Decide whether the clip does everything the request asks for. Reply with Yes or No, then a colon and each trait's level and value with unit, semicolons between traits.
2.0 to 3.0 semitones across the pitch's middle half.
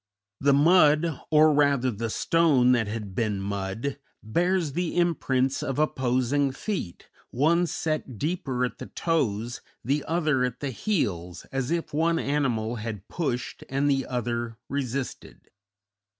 No: average, 4.7 semitones